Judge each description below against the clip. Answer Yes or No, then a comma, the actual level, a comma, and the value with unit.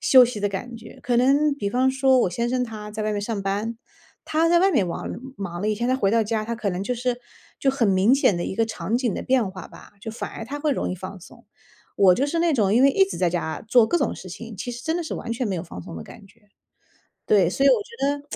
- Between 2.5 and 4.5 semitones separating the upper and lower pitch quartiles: No, average, 4.9 semitones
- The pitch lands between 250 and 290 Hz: No, high, 230 Hz